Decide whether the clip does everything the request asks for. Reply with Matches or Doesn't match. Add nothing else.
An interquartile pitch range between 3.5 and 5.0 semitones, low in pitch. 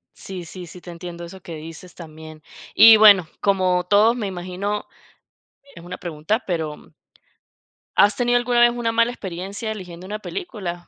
Doesn't match